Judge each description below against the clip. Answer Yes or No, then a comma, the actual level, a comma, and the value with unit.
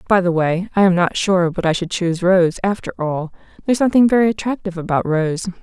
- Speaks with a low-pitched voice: No, medium, 185 Hz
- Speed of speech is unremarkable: No, fast, 215 wpm